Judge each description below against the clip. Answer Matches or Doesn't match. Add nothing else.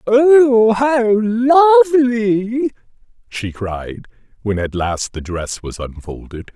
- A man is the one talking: Matches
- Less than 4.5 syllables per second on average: Matches